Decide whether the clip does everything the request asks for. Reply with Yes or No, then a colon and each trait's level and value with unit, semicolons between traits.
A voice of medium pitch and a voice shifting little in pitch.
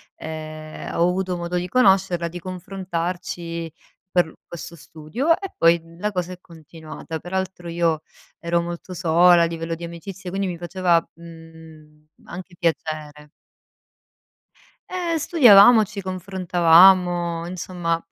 Yes: medium, 175 Hz; narrow, 1.9 semitones